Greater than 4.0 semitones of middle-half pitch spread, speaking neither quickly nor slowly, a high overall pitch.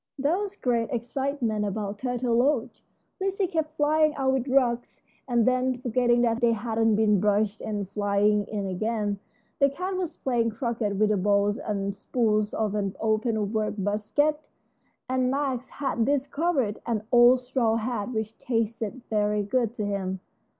No: average, 3.7 semitones; average, 155 wpm; high, 230 Hz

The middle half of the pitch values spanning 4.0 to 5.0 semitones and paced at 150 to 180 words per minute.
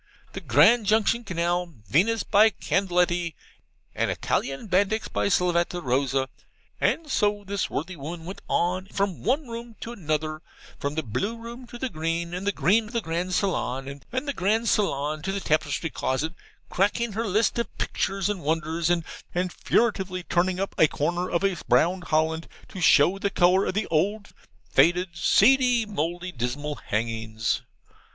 Yes: average, 4.6 semitones; average, 160 wpm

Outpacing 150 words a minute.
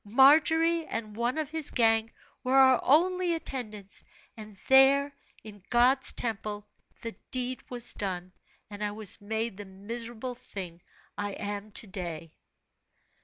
No: slow, 135 wpm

